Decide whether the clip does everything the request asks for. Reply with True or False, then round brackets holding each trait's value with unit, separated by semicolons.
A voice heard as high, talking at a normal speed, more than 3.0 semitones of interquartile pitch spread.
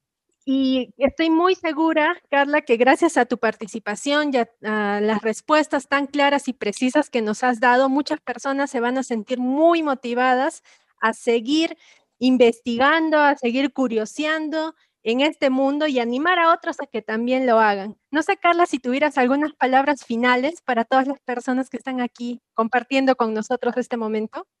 True (265 Hz; 170 wpm; 3.9 semitones)